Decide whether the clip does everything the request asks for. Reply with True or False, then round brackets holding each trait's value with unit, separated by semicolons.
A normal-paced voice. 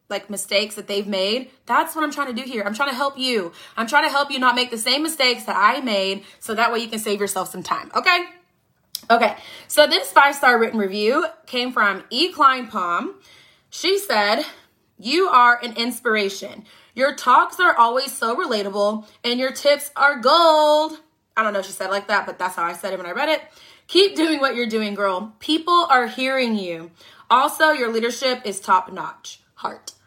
False (210 wpm)